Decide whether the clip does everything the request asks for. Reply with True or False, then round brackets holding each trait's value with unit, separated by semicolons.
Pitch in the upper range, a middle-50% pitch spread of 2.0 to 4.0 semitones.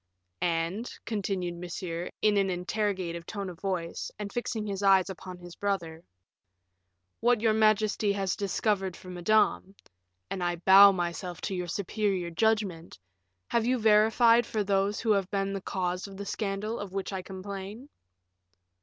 True (195 Hz; 2.8 semitones)